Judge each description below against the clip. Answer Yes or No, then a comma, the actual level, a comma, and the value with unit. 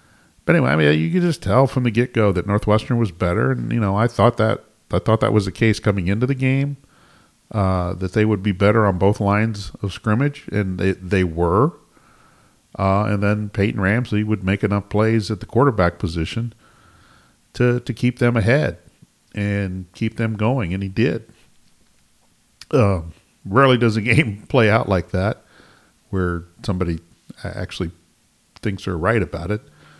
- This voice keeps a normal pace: Yes, average, 175 wpm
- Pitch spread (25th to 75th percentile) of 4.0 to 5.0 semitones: No, average, 3.4 semitones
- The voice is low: Yes, low, 105 Hz